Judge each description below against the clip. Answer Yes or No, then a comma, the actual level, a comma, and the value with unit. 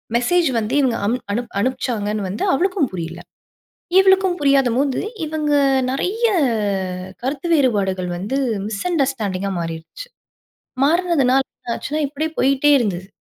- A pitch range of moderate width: No, wide, 6.4 semitones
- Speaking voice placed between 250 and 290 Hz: Yes, very high, 260 Hz